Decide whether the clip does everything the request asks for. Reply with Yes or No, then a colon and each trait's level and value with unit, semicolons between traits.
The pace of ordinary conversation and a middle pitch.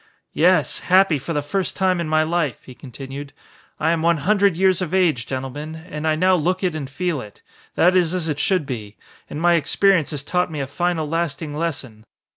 No: fast, 210 wpm; medium, 160 Hz